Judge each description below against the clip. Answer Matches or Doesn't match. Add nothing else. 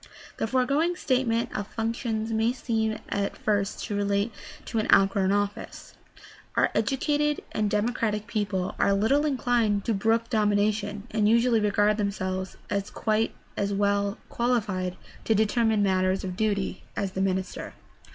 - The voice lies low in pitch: Doesn't match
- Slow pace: Doesn't match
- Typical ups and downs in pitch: Doesn't match